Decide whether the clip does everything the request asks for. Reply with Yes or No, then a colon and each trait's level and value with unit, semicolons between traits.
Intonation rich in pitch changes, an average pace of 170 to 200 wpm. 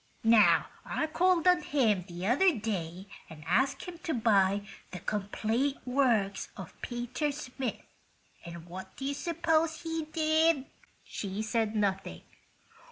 No: wide, 7.9 semitones; slow, 135 wpm